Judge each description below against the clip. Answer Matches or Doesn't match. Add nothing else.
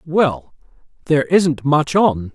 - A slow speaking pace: Matches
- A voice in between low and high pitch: Matches